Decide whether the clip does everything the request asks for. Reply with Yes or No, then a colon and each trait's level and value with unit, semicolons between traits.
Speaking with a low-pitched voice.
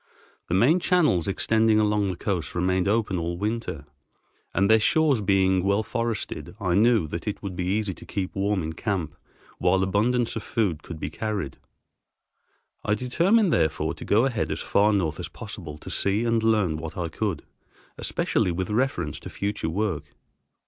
Yes: low, 100 Hz